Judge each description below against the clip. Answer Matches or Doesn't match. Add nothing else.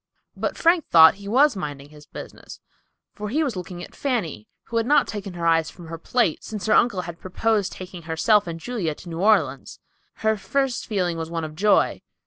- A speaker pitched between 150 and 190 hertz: Matches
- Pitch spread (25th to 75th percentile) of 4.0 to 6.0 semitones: Matches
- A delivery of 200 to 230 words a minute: Matches